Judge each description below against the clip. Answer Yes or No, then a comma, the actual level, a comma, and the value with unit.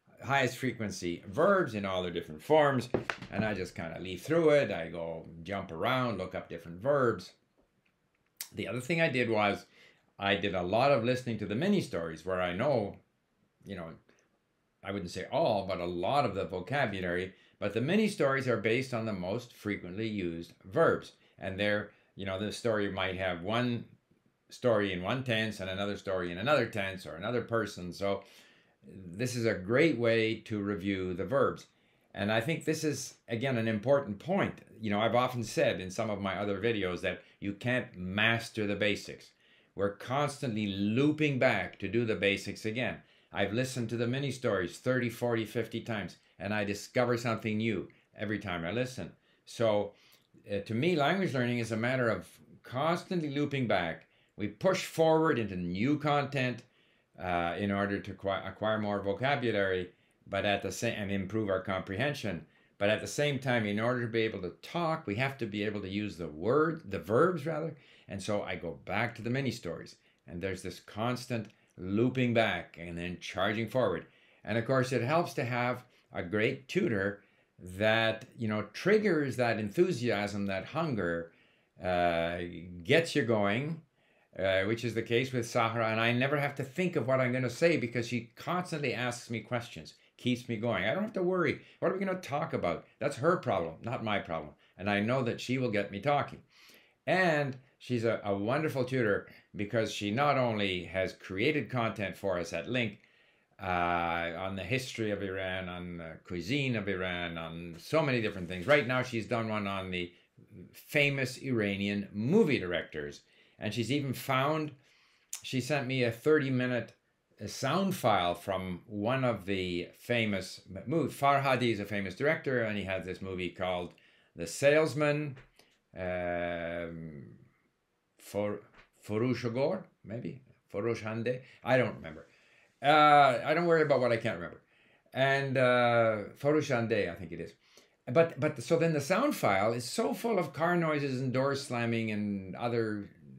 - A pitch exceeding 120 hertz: No, low, 115 Hz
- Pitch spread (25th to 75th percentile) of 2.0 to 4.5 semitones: No, average, 5.0 semitones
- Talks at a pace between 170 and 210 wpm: Yes, average, 175 wpm